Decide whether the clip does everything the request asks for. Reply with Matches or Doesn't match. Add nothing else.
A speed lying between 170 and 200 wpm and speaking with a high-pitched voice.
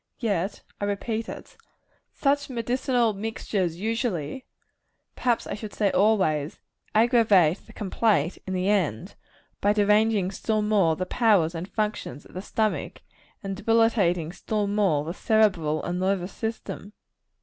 Doesn't match